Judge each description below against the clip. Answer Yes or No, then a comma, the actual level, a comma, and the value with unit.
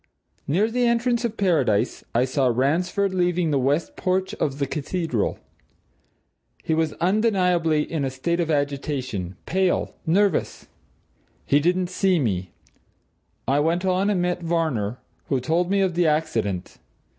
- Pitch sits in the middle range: Yes, medium, 165 Hz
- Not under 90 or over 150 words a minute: Yes, average, 145 wpm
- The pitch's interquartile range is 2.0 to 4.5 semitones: No, average, 4.9 semitones